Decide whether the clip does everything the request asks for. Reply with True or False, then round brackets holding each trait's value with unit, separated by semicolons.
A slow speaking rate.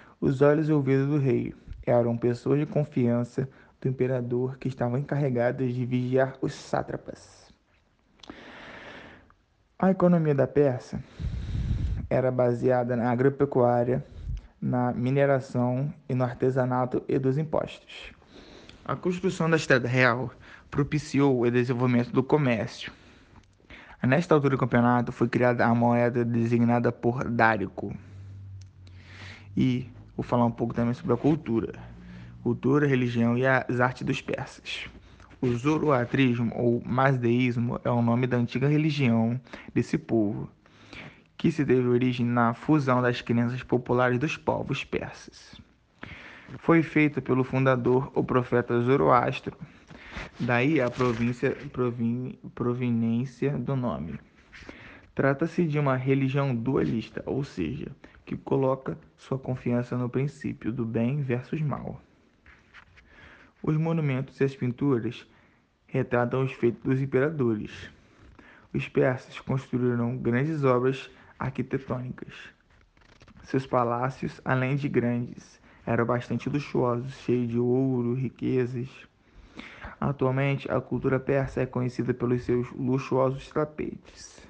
True (115 wpm)